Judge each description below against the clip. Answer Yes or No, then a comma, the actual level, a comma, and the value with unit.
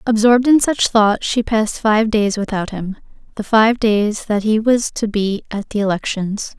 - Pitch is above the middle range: Yes, high, 215 Hz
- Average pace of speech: Yes, average, 190 wpm